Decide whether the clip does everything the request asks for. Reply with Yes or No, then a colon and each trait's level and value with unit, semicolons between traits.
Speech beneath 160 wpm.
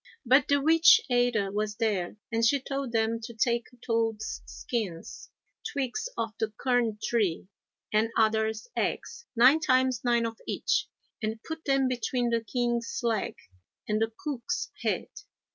Yes: average, 145 wpm